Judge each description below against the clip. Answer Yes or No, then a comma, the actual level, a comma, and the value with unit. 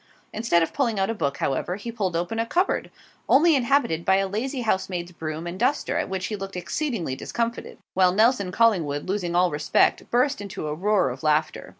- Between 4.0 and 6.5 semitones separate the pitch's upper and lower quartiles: Yes, average, 5.2 semitones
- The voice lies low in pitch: No, high, 195 Hz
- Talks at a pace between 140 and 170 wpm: No, average, 200 wpm